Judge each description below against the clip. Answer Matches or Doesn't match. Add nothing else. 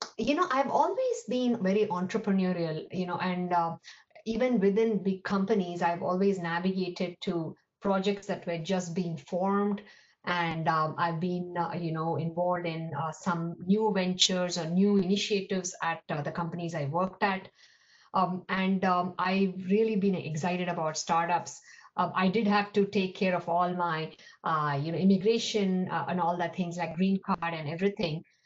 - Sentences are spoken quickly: Doesn't match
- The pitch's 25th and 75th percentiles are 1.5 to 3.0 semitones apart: Matches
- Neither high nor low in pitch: Matches